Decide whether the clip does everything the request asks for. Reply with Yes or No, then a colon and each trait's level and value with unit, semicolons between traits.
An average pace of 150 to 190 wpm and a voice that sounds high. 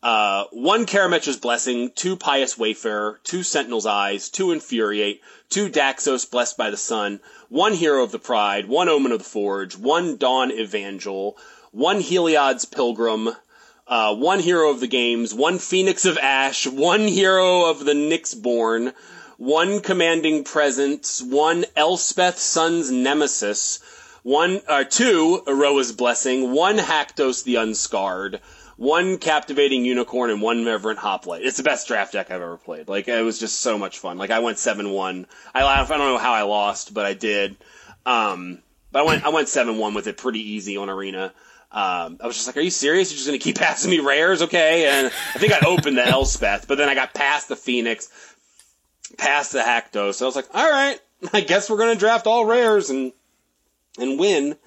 No: average, 180 wpm; low, 135 Hz